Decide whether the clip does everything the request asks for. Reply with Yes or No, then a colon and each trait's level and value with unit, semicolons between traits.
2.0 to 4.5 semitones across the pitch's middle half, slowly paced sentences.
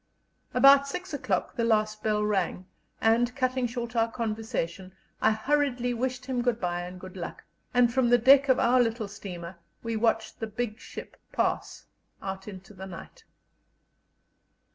No: average, 3.7 semitones; average, 160 wpm